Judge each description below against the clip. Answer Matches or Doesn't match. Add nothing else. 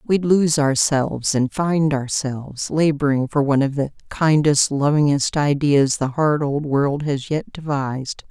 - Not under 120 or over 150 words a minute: Matches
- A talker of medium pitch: Matches